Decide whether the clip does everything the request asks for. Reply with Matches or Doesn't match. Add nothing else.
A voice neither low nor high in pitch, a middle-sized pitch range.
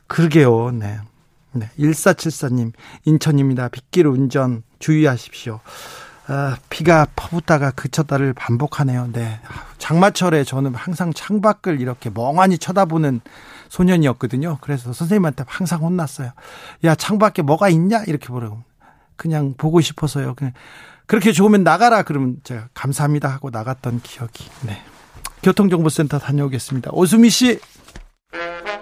Matches